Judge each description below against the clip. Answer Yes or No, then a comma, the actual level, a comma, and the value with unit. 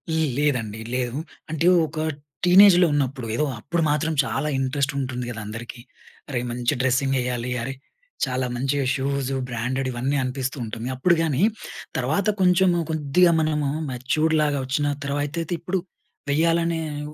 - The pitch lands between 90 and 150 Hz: Yes, medium, 140 Hz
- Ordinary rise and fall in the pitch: Yes, average, 3.8 semitones